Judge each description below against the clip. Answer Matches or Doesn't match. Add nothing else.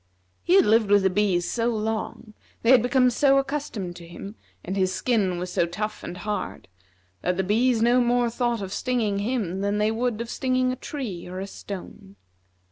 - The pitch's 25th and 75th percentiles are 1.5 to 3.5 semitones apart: Doesn't match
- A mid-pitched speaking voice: Doesn't match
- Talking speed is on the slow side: Doesn't match